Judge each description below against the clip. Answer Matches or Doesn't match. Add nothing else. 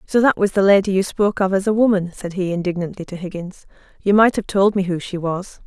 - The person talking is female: Matches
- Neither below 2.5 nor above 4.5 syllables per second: Doesn't match